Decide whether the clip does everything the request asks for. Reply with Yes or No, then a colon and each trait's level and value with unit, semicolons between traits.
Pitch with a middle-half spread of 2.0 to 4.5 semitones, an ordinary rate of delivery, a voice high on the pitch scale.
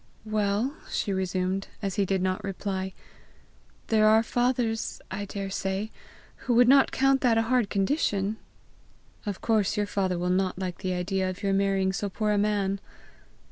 Yes: narrow, 2.5 semitones; average, 165 wpm; high, 200 Hz